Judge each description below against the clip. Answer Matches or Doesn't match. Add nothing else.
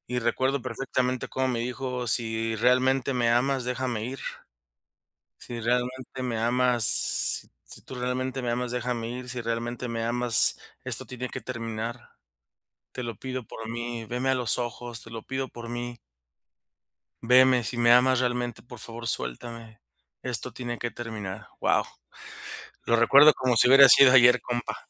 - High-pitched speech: Doesn't match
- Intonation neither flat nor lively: Doesn't match